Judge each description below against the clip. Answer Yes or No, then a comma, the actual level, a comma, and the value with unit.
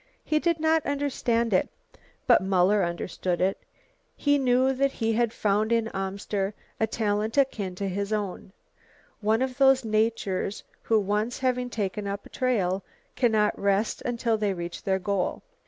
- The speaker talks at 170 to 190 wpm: No, average, 155 wpm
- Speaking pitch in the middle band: No, high, 215 Hz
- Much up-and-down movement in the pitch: No, average, 4.0 semitones